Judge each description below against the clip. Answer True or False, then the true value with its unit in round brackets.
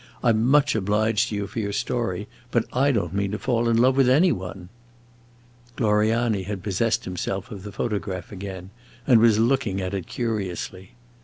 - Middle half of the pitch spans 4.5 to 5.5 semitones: False (3.5 semitones)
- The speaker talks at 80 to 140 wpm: False (180 wpm)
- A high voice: False (105 Hz)